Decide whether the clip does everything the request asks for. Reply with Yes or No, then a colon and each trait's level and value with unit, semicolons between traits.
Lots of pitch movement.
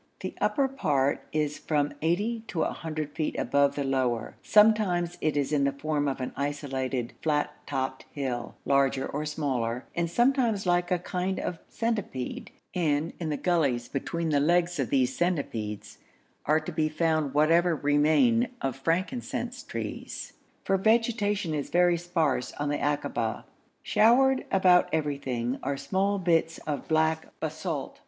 No: average, 4.2 semitones